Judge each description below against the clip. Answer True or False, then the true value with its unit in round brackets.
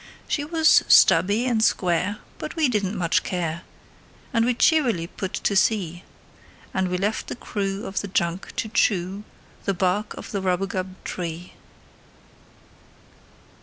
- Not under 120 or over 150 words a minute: True (140 wpm)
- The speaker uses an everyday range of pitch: True (3.4 semitones)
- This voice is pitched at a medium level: False (195 Hz)